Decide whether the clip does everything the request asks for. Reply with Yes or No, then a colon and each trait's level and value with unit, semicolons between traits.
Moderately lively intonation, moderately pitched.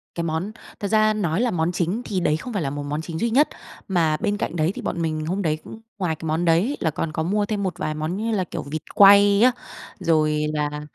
Yes: average, 4.5 semitones; medium, 170 Hz